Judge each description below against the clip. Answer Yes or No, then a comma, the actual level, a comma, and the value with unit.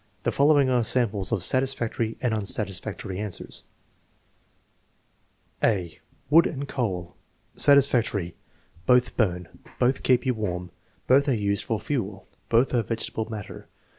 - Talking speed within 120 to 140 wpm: Yes, slow, 135 wpm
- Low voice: Yes, low, 115 Hz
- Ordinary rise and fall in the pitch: Yes, average, 4.5 semitones